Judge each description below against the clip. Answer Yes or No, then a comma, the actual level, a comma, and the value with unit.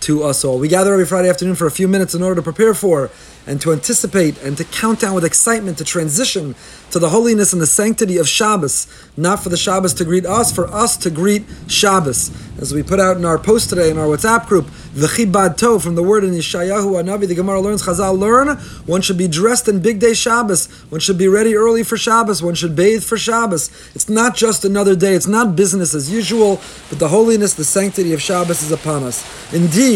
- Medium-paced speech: No, fast, 230 wpm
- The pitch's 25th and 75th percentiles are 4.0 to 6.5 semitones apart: Yes, average, 4.3 semitones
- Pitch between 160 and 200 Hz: Yes, high, 190 Hz